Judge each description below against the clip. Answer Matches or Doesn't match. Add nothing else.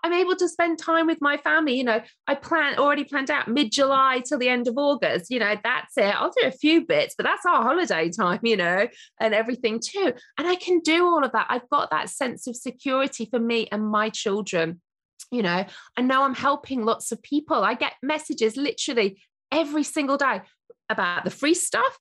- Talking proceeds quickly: Matches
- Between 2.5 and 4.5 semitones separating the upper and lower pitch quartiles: Doesn't match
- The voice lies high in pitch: Matches